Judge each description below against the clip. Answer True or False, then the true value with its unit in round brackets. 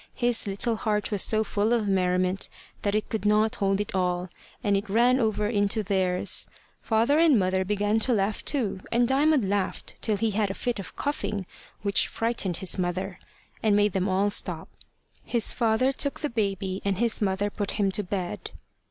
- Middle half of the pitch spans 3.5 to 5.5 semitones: False (2.7 semitones)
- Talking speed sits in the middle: True (185 wpm)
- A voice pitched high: True (205 Hz)